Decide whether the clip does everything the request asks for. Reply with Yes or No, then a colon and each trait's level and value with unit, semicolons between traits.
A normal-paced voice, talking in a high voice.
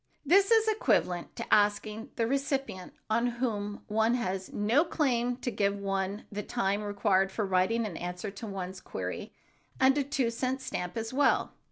Yes: average, 170 wpm; high, 220 Hz